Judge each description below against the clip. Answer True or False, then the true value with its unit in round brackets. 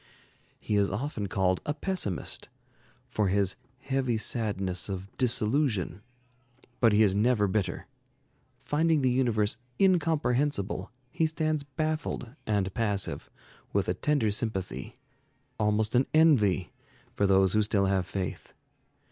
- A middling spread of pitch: False (5.9 semitones)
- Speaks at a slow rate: True (120 wpm)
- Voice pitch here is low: True (110 Hz)